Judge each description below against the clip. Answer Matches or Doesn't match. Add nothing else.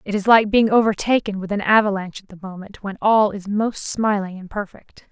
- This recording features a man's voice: Doesn't match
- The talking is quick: Matches